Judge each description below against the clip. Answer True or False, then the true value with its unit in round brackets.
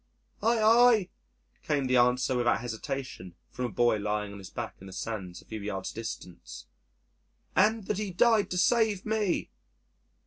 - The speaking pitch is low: True (125 Hz)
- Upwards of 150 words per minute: True (165 wpm)